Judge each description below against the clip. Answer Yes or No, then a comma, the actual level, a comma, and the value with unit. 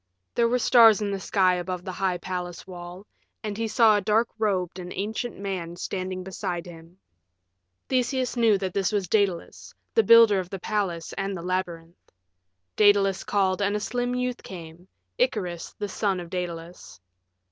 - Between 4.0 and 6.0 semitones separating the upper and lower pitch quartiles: No, average, 3.0 semitones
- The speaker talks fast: No, average, 170 wpm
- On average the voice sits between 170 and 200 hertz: Yes, high, 190 Hz